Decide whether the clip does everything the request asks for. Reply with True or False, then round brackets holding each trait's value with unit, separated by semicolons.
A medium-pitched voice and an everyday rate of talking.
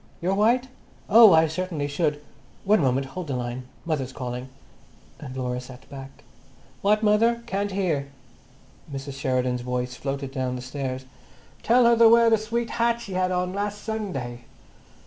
True (155 Hz; 155 wpm)